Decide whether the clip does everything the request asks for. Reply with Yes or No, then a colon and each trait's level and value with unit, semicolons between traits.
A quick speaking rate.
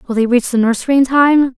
Yes: fast, 265 wpm